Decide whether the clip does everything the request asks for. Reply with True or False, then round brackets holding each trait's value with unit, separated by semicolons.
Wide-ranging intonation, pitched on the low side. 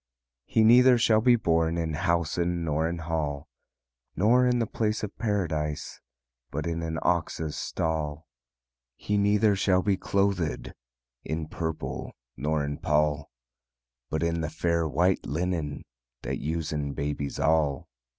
False (4.4 semitones; 80 Hz)